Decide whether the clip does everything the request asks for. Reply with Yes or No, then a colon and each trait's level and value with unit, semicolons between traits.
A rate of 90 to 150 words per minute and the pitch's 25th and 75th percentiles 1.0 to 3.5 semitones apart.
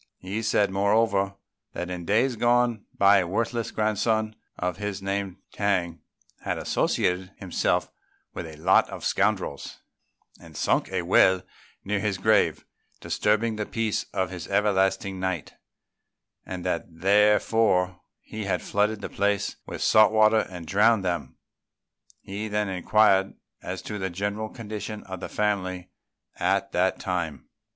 Yes: average, 140 wpm; narrow, 2.5 semitones